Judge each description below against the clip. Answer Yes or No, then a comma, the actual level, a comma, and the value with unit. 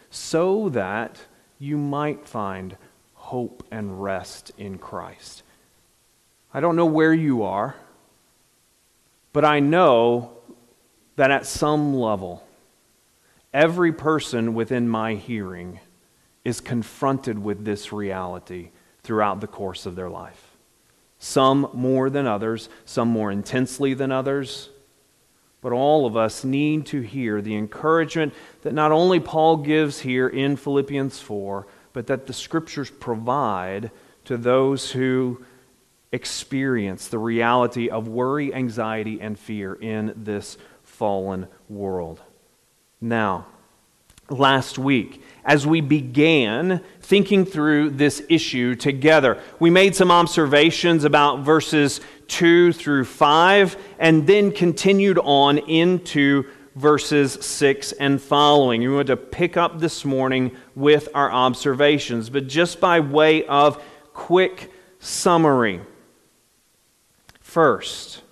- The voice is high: No, low, 135 Hz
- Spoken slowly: Yes, slow, 115 wpm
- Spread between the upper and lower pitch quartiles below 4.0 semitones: No, average, 4.8 semitones